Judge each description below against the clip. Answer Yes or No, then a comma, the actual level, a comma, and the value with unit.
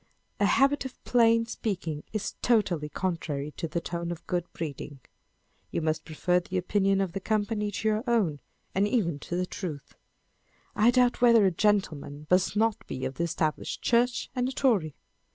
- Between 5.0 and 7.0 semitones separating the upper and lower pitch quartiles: Yes, wide, 5.4 semitones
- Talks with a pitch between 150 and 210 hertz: Yes, high, 190 Hz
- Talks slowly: No, average, 170 wpm